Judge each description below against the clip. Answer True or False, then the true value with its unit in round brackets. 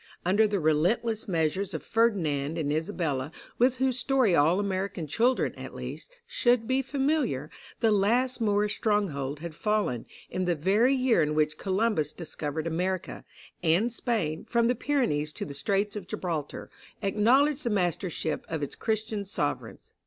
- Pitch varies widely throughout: True (6.6 semitones)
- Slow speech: False (155 wpm)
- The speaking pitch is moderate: False (195 Hz)